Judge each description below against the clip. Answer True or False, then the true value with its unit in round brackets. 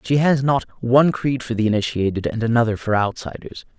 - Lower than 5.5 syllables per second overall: False (5.9 syllables/s)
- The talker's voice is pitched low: True (120 Hz)